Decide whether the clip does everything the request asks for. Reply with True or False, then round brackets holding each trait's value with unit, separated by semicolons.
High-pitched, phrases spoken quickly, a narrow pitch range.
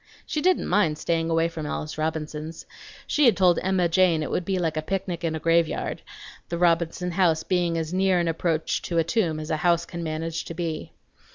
False (170 Hz; 210 wpm; 2.0 semitones)